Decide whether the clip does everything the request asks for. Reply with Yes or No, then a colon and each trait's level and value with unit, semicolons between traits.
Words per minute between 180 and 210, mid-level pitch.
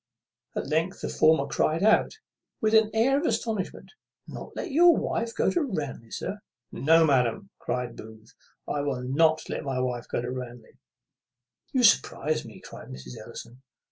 No: average, 165 wpm; medium, 155 Hz